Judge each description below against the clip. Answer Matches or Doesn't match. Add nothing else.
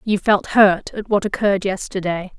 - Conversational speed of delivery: Matches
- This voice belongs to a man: Doesn't match